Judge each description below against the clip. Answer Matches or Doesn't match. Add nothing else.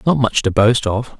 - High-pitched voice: Doesn't match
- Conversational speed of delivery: Doesn't match